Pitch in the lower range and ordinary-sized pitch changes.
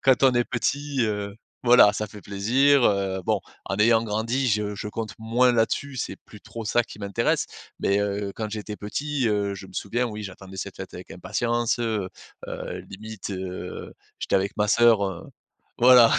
Yes: low, 105 Hz; average, 3.0 semitones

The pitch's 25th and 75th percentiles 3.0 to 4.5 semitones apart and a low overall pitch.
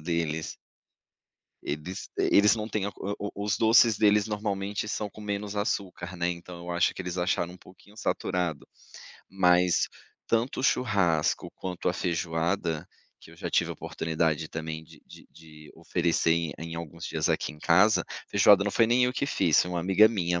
Yes: average, 3.7 semitones; very low, 90 Hz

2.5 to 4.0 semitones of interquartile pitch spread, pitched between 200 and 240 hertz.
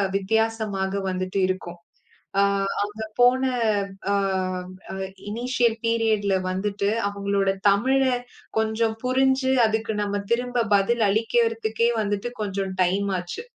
Yes: average, 2.9 semitones; high, 220 Hz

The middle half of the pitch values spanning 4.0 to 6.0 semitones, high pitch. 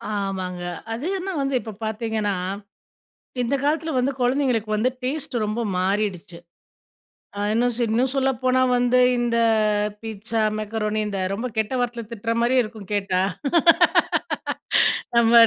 No: average, 3.1 semitones; high, 230 Hz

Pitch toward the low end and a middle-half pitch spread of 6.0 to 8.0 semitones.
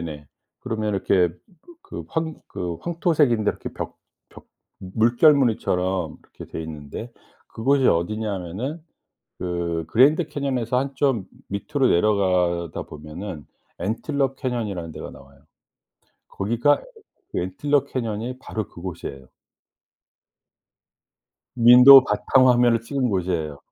Yes: low, 110 Hz; wide, 6.9 semitones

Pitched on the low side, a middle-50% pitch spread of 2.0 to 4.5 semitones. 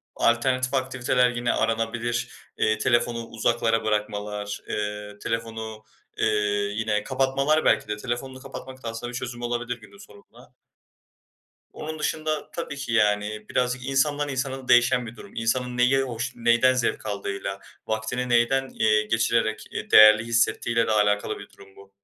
Yes: low, 120 Hz; average, 2.9 semitones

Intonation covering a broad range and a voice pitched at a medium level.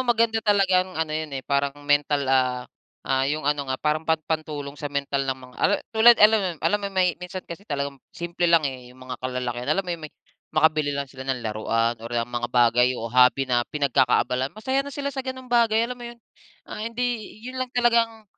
Yes: wide, 8.4 semitones; medium, 155 Hz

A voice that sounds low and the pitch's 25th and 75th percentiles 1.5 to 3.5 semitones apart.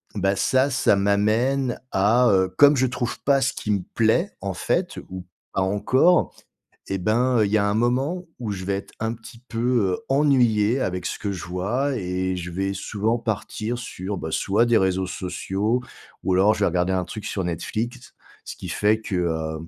No: low, 105 Hz; average, 4.5 semitones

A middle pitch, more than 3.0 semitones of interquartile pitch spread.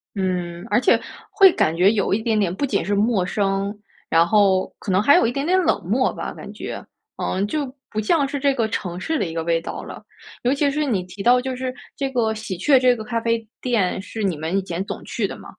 No: high, 215 Hz; average, 5.3 semitones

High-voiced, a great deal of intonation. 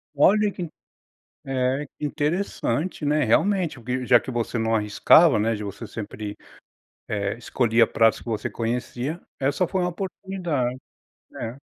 No: low, 130 Hz; wide, 6.4 semitones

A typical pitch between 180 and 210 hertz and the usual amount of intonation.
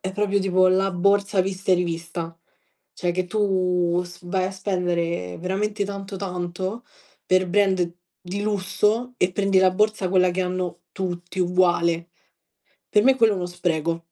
No: medium, 185 Hz; narrow, 2.0 semitones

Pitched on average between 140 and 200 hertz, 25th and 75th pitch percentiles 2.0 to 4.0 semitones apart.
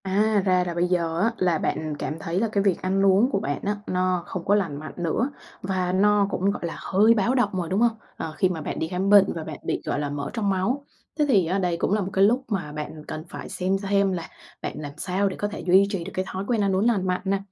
Yes: high, 190 Hz; average, 2.7 semitones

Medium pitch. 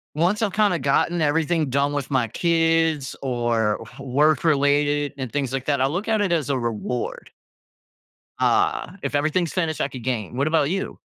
Yes: medium, 145 Hz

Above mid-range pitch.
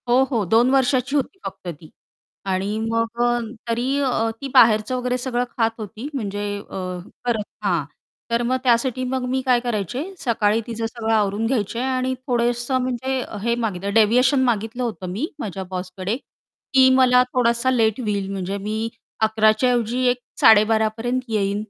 Yes: high, 230 Hz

